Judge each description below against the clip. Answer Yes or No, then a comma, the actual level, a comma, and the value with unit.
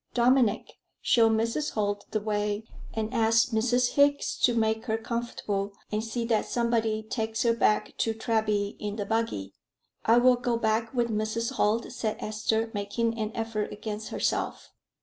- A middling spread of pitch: No, narrow, 1.5 semitones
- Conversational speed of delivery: Yes, average, 160 wpm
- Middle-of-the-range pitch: No, high, 225 Hz